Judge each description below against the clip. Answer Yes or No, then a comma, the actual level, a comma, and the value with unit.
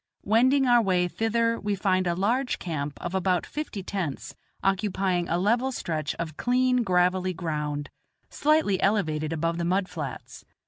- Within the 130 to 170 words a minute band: Yes, average, 150 wpm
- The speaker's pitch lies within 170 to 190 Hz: Yes, medium, 185 Hz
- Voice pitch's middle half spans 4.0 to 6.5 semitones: Yes, average, 4.9 semitones